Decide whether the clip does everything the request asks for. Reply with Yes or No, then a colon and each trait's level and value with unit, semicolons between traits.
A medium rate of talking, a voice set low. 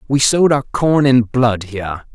Yes: average, 195 wpm; low, 125 Hz